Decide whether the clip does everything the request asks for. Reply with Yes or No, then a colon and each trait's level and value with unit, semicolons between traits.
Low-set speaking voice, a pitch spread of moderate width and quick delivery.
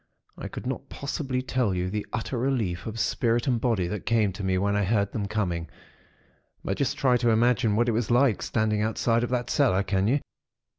Yes: low, 110 Hz; average, 3.4 semitones; fast, 210 wpm